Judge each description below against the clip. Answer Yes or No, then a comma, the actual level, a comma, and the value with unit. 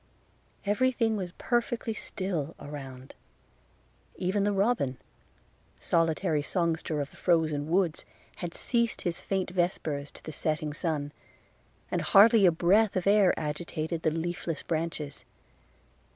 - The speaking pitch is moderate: Yes, medium, 170 Hz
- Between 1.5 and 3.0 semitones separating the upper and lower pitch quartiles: No, average, 4.2 semitones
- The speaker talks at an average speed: No, slow, 125 wpm